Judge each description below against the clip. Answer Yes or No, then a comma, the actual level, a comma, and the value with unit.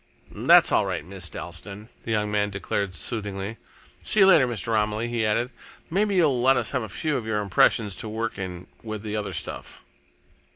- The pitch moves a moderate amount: Yes, average, 3.0 semitones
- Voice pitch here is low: Yes, low, 110 Hz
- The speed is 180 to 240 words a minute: Yes, average, 195 wpm